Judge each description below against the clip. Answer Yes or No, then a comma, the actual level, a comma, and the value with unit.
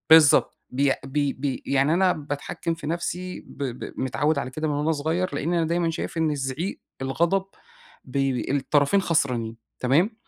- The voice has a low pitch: No, medium, 145 Hz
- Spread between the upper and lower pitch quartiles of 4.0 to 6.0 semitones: No, average, 3.6 semitones